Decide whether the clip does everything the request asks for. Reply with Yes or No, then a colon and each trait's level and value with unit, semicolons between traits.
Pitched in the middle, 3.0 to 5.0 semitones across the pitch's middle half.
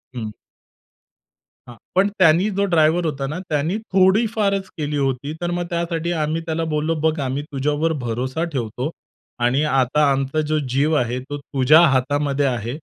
Yes: medium, 150 Hz; average, 3.7 semitones